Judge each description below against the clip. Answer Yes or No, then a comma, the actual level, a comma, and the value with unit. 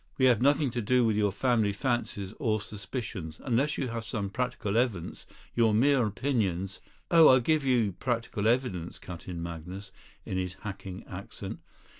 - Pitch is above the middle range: No, low, 110 Hz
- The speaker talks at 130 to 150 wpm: No, average, 170 wpm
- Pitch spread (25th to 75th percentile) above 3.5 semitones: Yes, average, 4.6 semitones